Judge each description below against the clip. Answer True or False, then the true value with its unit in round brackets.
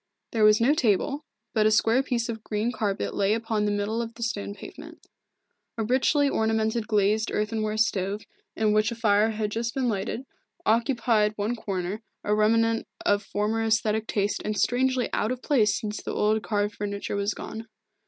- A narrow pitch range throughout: True (1.7 semitones)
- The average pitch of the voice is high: True (220 Hz)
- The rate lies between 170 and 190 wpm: True (180 wpm)